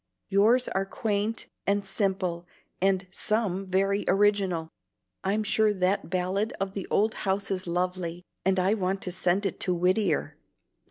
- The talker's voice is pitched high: Yes, high, 195 Hz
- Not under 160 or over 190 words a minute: No, average, 150 wpm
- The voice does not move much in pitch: Yes, narrow, 1.9 semitones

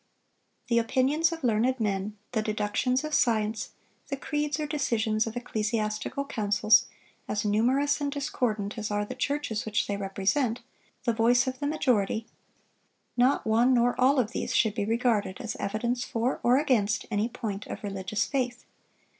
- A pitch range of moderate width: Yes, average, 3.5 semitones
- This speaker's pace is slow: No, average, 155 wpm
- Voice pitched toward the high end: Yes, high, 230 Hz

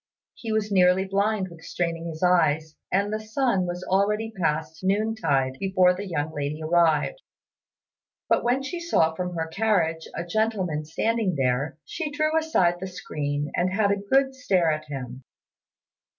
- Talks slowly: No, average, 160 wpm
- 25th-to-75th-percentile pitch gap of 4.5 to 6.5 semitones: Yes, average, 5.3 semitones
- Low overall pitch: No, medium, 180 Hz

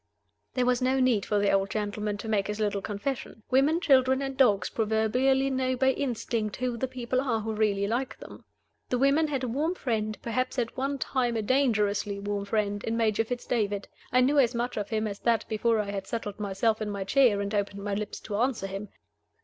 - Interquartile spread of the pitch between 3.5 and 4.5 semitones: Yes, average, 3.9 semitones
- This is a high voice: Yes, high, 225 Hz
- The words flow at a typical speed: No, fast, 215 wpm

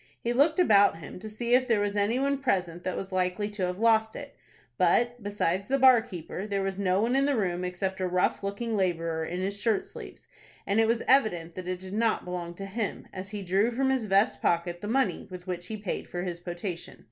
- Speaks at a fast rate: Yes, fast, 235 wpm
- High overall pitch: Yes, high, 200 Hz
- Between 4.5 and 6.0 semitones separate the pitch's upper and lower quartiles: No, average, 3.9 semitones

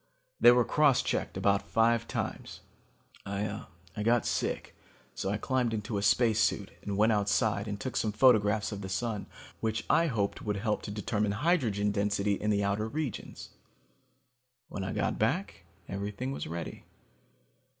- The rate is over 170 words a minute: No, average, 155 wpm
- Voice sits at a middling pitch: No, low, 105 Hz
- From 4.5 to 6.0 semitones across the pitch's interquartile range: No, narrow, 2.5 semitones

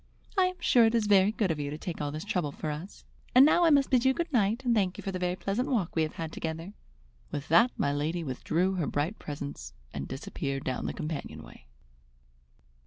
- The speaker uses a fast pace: Yes, fast, 235 wpm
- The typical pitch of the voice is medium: Yes, medium, 180 Hz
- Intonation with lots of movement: Yes, wide, 7.1 semitones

